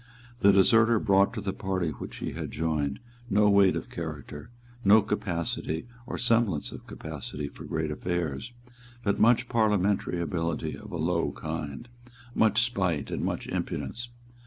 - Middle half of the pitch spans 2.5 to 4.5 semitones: No, average, 5.0 semitones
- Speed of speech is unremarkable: Yes, average, 150 wpm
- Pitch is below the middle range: Yes, very low, 95 Hz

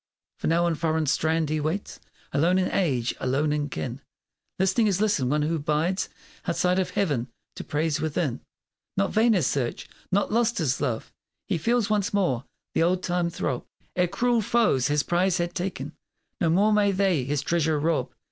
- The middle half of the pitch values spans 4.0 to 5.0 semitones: Yes, average, 4.5 semitones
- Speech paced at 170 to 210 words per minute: Yes, average, 180 wpm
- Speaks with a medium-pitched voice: Yes, medium, 170 Hz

